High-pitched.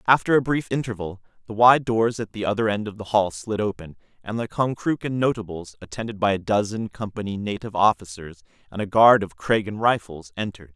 No: low, 105 Hz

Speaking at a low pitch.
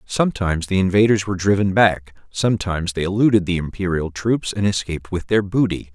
Yes: very low, 95 Hz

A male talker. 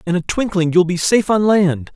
Yes: male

